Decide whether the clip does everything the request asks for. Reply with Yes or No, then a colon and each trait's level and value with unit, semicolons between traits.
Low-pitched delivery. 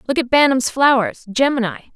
No: very high, 255 Hz